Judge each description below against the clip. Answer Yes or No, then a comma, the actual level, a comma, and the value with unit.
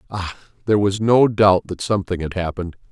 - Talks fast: No, average, 185 wpm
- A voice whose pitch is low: Yes, very low, 95 Hz